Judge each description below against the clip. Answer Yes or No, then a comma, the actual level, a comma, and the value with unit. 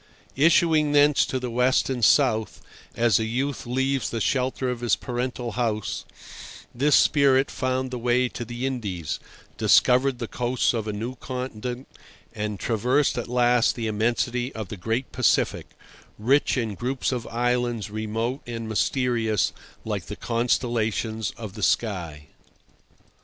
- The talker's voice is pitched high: No, low, 120 Hz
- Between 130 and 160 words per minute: Yes, average, 145 wpm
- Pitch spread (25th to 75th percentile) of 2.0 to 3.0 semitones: Yes, narrow, 2.6 semitones